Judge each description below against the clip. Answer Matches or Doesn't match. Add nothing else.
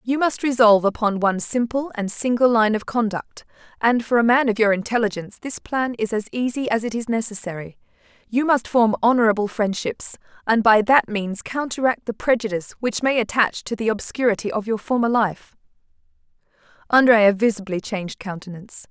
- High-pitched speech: Matches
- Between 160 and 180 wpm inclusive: Matches